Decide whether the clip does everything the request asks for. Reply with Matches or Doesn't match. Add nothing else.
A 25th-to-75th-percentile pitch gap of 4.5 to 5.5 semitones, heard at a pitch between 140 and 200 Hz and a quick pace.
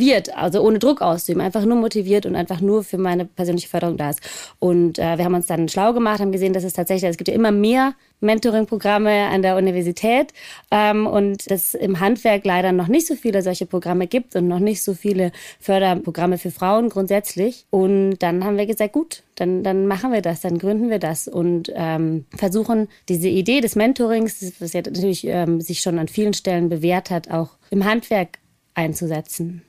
Doesn't match